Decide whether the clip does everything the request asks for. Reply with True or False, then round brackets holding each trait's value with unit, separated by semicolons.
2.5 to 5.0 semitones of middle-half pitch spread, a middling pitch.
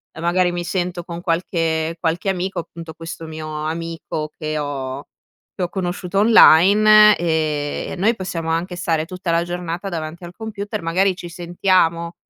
False (2.1 semitones; 170 Hz)